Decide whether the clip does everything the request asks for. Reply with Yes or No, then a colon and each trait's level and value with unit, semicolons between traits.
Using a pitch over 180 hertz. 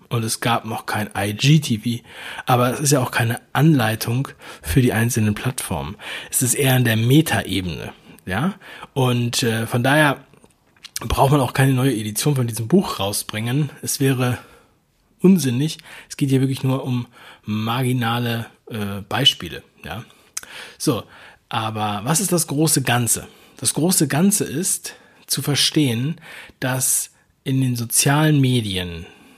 No: low, 130 Hz